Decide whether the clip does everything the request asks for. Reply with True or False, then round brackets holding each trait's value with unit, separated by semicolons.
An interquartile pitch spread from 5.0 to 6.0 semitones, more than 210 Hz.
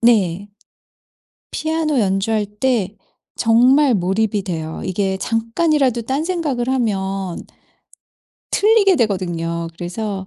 True (5.6 semitones; 220 Hz)